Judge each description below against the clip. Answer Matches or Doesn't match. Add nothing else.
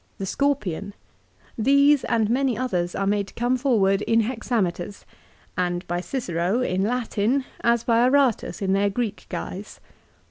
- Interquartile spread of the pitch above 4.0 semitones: Matches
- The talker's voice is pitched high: Matches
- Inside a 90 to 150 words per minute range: Matches